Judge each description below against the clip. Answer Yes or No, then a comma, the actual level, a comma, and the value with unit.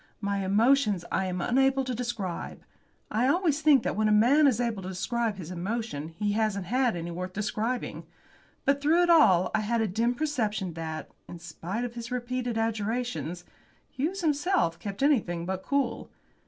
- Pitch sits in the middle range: No, high, 225 Hz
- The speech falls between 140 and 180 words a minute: Yes, average, 175 wpm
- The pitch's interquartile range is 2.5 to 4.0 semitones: No, average, 5.2 semitones